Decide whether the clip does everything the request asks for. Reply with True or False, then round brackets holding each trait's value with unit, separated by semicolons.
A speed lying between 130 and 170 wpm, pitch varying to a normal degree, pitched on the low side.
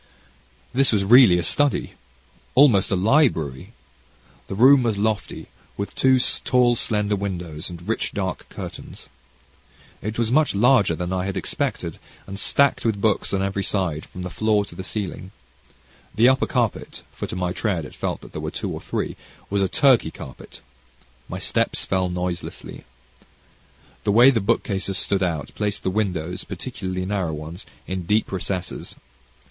True (160 wpm; 3.8 semitones; 100 Hz)